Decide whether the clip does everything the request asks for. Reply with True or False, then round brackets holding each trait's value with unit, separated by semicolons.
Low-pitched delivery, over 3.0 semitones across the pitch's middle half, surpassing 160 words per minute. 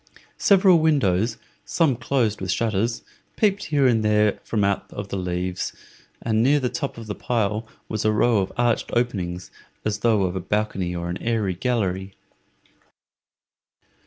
False (110 Hz; 4.1 semitones; 155 wpm)